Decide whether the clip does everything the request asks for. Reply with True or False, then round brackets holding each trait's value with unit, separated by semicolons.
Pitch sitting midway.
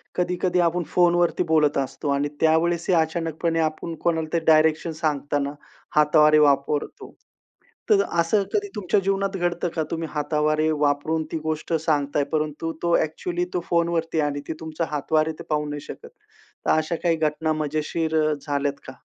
True (160 Hz)